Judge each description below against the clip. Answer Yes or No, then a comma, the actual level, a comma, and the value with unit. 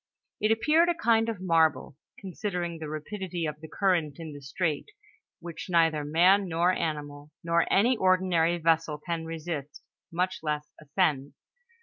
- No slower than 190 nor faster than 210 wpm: No, average, 145 wpm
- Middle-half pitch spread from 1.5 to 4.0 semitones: Yes, average, 3.4 semitones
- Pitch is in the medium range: Yes, medium, 165 Hz